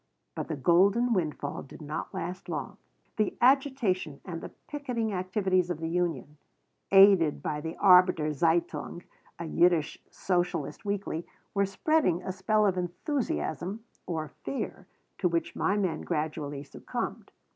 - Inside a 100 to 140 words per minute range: Yes, slow, 135 wpm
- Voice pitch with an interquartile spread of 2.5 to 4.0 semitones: Yes, average, 3.6 semitones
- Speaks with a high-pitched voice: No, medium, 180 Hz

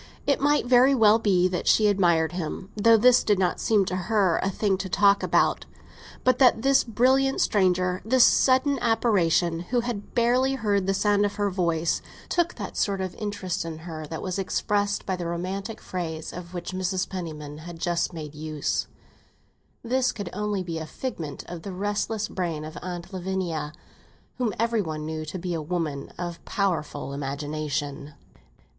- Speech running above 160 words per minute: Yes, average, 170 wpm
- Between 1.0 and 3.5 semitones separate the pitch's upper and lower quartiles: No, average, 4.3 semitones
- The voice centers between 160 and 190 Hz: Yes, medium, 185 Hz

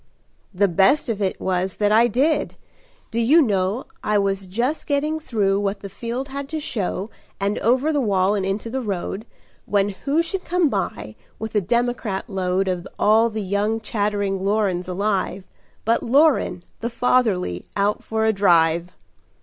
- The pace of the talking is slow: No, average, 165 wpm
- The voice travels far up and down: No, average, 3.9 semitones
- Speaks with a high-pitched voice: Yes, high, 210 Hz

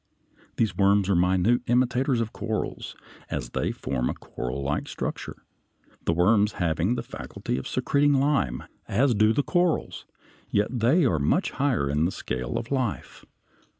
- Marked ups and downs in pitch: Yes, wide, 6.7 semitones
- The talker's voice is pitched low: Yes, low, 110 Hz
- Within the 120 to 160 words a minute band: Yes, average, 150 wpm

